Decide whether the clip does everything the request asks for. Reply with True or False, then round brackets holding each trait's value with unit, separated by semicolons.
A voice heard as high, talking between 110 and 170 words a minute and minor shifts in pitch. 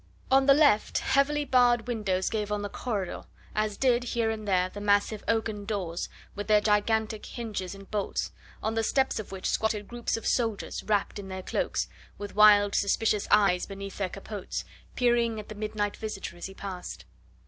False (210 Hz; 180 wpm; 2.2 semitones)